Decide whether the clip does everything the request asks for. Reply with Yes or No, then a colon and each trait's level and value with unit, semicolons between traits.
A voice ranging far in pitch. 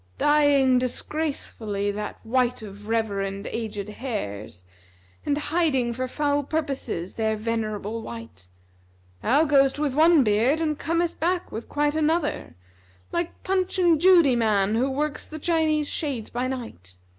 Yes: wide, 6.3 semitones